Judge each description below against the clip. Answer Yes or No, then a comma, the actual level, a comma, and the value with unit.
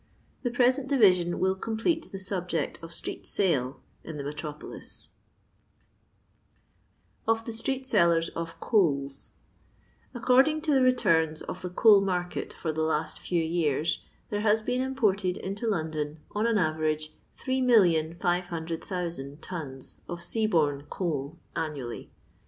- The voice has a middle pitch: Yes, medium, 175 Hz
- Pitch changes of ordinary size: No, wide, 5.9 semitones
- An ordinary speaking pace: No, slow, 130 wpm